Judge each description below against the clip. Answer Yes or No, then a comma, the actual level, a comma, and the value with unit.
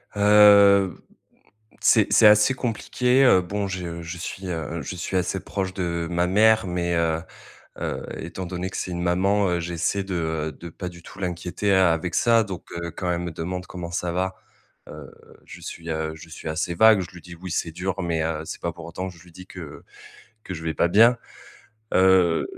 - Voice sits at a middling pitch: No, very low, 90 Hz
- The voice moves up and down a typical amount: No, narrow, 2.2 semitones